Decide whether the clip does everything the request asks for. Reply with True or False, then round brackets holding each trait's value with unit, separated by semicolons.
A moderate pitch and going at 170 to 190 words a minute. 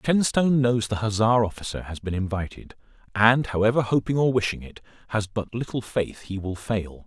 False (110 Hz; 180 wpm)